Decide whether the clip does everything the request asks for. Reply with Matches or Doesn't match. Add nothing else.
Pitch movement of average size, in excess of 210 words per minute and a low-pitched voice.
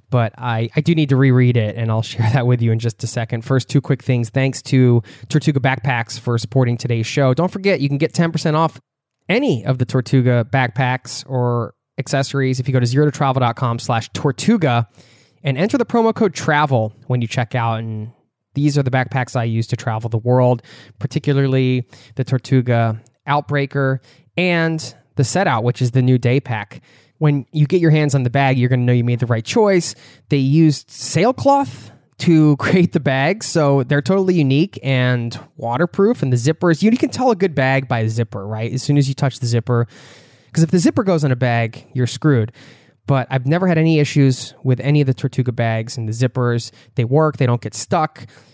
Doesn't match